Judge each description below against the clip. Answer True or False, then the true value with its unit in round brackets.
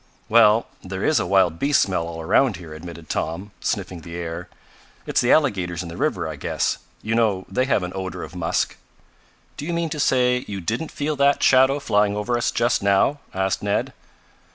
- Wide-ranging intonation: True (6.1 semitones)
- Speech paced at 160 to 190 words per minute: False (200 wpm)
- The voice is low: True (100 Hz)